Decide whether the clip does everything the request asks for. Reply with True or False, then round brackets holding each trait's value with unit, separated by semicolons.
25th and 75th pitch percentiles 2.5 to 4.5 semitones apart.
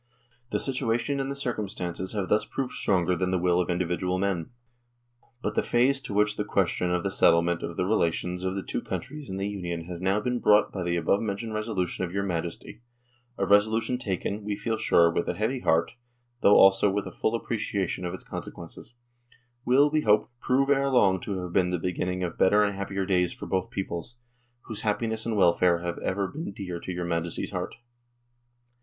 True (3.7 semitones)